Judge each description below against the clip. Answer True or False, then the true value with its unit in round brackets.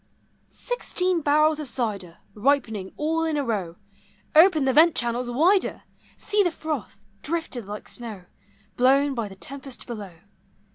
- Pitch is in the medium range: False (270 Hz)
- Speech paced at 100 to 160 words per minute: True (140 wpm)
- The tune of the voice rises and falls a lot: True (5.9 semitones)